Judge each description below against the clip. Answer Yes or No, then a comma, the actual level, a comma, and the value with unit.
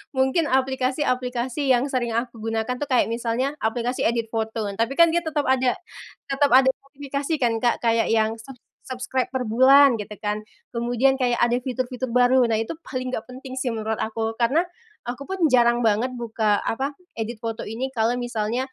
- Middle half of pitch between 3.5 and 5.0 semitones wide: No, narrow, 2.6 semitones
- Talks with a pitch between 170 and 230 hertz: No, high, 245 Hz